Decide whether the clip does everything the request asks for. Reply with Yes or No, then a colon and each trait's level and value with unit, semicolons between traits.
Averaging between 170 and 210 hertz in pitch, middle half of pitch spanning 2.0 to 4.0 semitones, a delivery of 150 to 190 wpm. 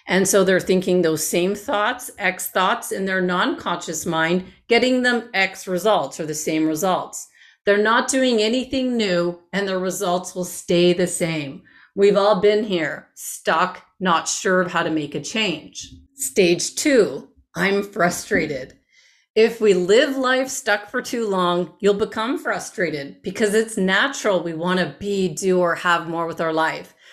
Yes: high, 190 Hz; average, 3.7 semitones; average, 170 wpm